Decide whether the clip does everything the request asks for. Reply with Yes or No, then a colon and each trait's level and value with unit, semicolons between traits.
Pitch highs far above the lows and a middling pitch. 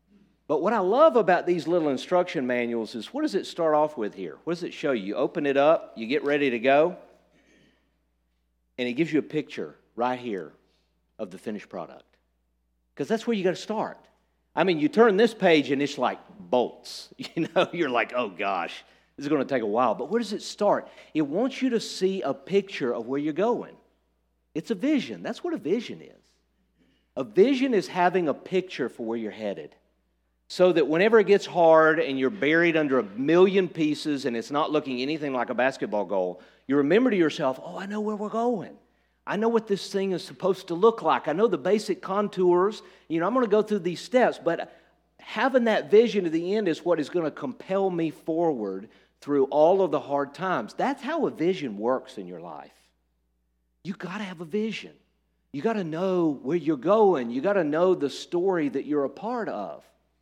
Yes: wide, 7.7 semitones; medium, 170 Hz